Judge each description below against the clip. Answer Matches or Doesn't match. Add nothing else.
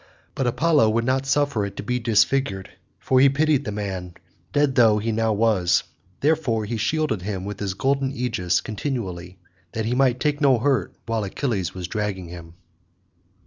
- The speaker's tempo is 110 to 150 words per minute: Doesn't match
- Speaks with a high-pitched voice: Doesn't match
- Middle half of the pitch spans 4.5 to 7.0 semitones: Matches